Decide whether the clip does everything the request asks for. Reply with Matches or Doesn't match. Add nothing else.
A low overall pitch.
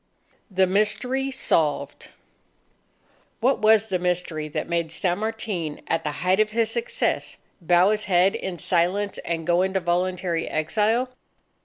Doesn't match